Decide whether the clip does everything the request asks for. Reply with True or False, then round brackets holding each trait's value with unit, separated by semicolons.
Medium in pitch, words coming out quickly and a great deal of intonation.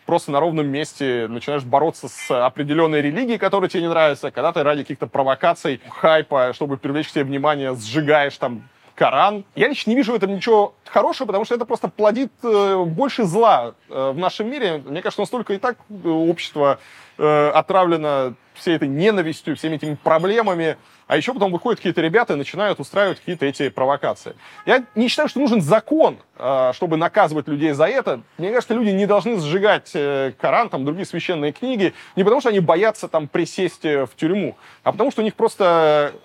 True (170 Hz; 175 wpm; 5.9 semitones)